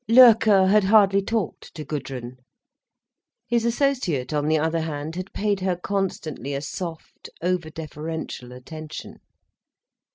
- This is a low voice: No, medium, 170 Hz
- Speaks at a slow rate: Yes, slow, 125 wpm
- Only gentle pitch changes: No, average, 4.9 semitones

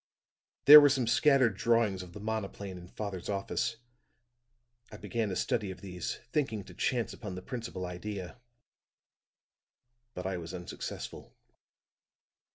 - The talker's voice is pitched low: Yes, low, 100 Hz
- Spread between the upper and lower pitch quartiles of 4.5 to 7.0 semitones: No, average, 4.1 semitones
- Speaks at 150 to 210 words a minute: No, slow, 135 wpm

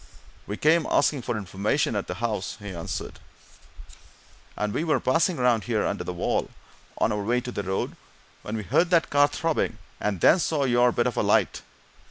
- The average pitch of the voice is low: Yes, low, 120 Hz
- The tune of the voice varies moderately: No, wide, 6.1 semitones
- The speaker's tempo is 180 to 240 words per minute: Yes, average, 195 wpm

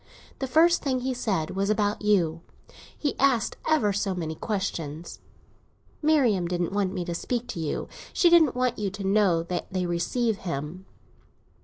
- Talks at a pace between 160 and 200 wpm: Yes, average, 165 wpm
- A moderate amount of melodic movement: No, wide, 6.1 semitones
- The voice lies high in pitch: Yes, high, 200 Hz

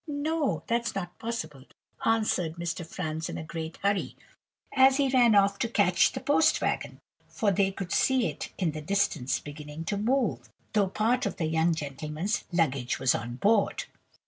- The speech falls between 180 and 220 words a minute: No, average, 170 wpm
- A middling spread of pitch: No, wide, 6.3 semitones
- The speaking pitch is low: No, high, 190 Hz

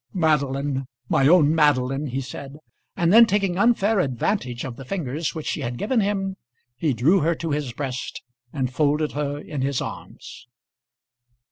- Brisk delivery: No, average, 160 wpm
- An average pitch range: Yes, average, 4.8 semitones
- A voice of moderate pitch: Yes, medium, 150 Hz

